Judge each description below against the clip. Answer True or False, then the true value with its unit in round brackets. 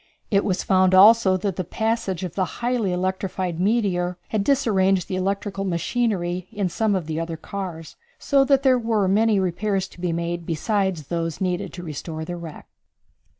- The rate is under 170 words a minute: False (175 wpm)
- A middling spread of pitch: True (3.0 semitones)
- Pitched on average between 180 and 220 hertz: True (190 Hz)